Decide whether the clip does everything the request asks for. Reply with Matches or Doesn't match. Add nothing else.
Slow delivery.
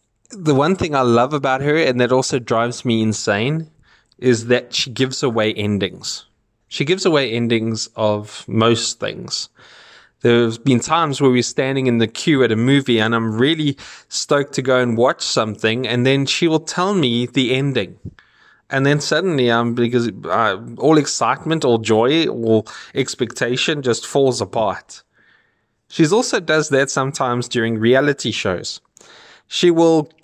Doesn't match